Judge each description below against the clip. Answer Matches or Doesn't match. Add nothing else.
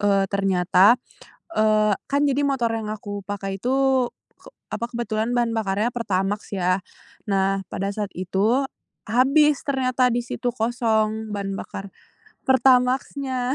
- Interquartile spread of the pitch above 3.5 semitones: Matches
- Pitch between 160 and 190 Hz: Doesn't match